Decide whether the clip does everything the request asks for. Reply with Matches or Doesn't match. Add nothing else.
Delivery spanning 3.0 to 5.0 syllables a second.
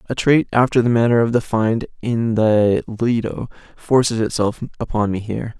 Matches